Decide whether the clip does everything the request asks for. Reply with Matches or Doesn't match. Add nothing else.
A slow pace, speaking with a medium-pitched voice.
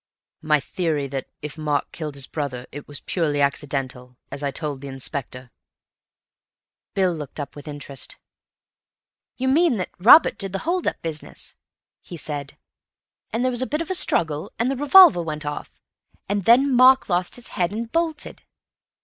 Doesn't match